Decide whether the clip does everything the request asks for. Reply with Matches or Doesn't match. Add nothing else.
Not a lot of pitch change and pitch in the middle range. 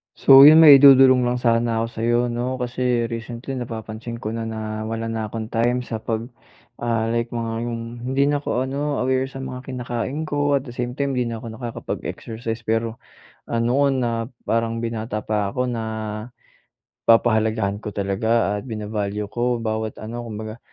Doesn't match